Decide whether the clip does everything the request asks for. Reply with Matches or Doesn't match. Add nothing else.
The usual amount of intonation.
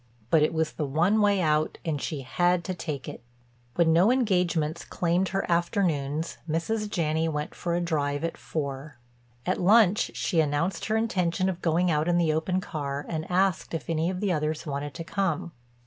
Matches